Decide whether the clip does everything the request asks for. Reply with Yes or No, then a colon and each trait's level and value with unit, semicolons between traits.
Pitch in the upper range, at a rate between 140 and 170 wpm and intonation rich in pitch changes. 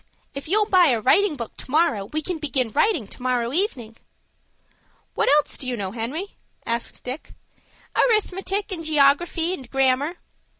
Yes: very high, 290 Hz; average, 160 wpm; wide, 6.2 semitones